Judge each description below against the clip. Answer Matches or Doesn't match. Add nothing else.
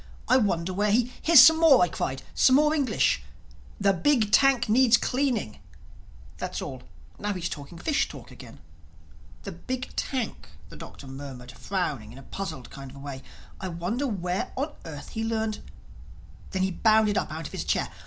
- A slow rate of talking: Doesn't match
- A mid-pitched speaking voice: Doesn't match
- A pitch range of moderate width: Doesn't match